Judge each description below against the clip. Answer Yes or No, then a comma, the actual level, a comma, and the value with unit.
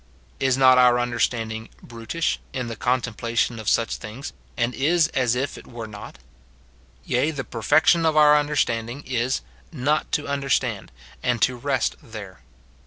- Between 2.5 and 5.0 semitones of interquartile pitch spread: Yes, average, 3.4 semitones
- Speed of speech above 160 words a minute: No, average, 155 wpm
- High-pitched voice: No, low, 125 Hz